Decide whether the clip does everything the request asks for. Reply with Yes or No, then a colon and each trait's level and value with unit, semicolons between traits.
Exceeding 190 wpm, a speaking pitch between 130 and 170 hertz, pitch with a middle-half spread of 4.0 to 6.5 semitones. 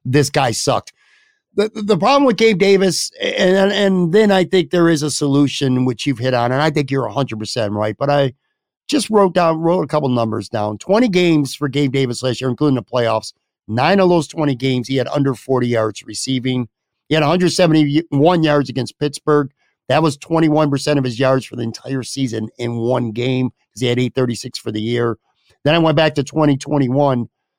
Yes: average, 200 wpm; medium, 140 Hz; average, 4.6 semitones